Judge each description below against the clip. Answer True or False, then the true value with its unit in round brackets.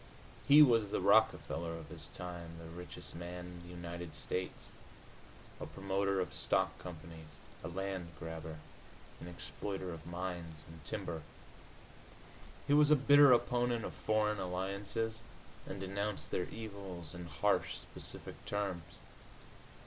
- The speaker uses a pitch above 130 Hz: False (90 Hz)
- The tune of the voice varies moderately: True (3.3 semitones)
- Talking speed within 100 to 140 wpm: True (135 wpm)